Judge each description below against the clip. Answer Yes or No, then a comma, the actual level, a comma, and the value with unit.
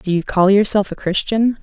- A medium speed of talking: No, fast, 220 wpm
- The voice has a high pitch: Yes, high, 200 Hz